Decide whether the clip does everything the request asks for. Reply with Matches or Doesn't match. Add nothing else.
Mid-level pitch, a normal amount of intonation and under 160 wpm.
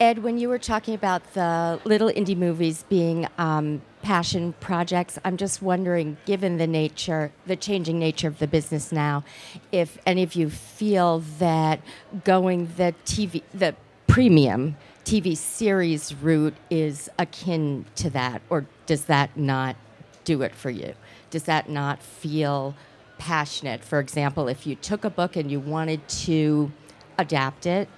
Matches